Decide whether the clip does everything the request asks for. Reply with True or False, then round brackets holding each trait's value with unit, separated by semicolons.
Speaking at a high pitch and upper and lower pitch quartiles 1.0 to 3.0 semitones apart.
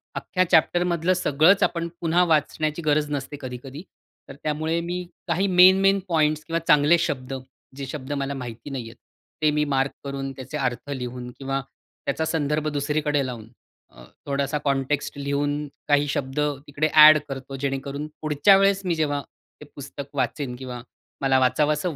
False (145 Hz; 2.5 semitones)